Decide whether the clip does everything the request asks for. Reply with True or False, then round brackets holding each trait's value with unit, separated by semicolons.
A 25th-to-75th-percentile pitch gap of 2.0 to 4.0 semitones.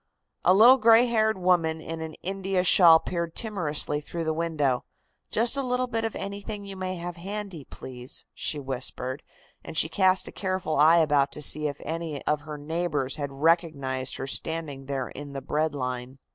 False (4.7 semitones)